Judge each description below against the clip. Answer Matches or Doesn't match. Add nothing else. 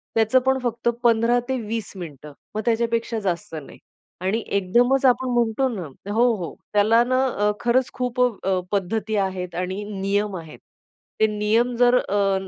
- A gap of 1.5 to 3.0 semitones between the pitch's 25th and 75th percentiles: Doesn't match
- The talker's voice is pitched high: Matches